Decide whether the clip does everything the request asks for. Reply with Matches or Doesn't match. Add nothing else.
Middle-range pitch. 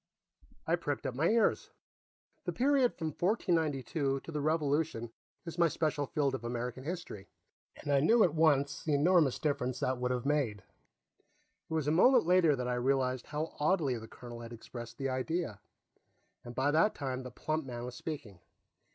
Matches